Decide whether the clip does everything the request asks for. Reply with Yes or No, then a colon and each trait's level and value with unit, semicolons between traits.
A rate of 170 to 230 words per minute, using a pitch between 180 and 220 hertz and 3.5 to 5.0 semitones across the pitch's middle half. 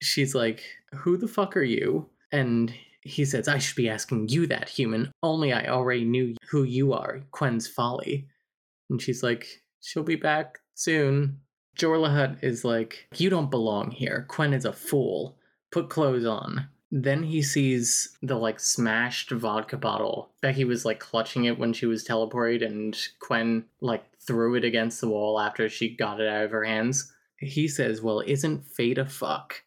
No: average, 180 wpm; low, 125 Hz; average, 3.8 semitones